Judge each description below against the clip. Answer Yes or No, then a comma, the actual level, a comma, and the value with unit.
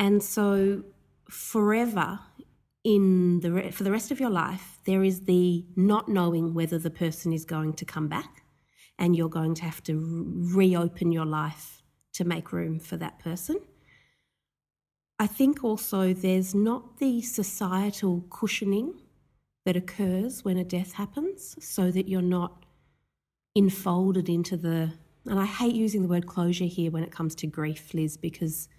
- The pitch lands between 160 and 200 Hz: Yes, medium, 185 Hz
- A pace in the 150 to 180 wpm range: Yes, average, 160 wpm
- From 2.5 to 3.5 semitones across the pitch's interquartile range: Yes, average, 3.2 semitones